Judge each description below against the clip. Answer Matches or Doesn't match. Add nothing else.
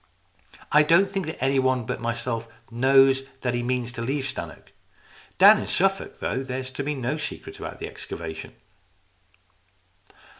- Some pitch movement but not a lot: Matches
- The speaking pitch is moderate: Doesn't match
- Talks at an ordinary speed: Matches